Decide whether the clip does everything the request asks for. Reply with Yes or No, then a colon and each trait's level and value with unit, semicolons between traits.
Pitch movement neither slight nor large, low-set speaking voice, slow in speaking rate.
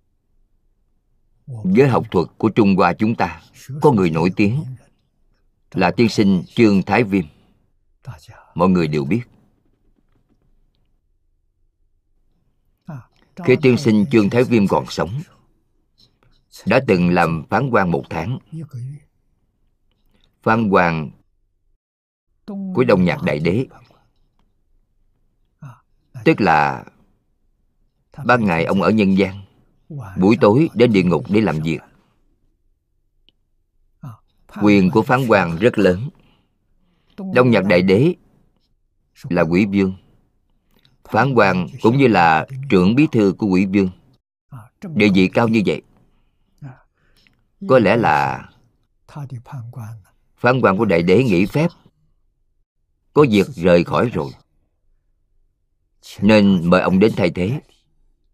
No: wide, 5.8 semitones; low, 100 Hz; slow, 115 wpm